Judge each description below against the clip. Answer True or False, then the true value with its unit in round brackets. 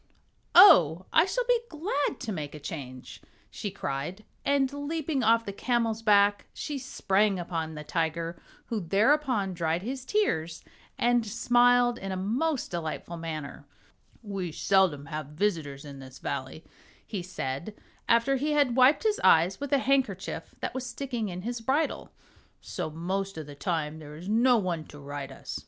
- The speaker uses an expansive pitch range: True (7.7 semitones)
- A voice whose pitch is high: True (195 Hz)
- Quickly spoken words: False (165 wpm)